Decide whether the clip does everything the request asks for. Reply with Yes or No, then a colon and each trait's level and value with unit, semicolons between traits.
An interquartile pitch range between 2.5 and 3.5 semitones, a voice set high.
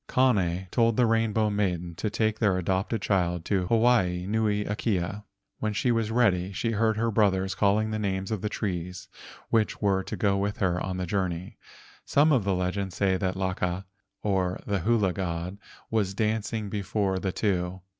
No: average, 2.9 semitones; low, 100 Hz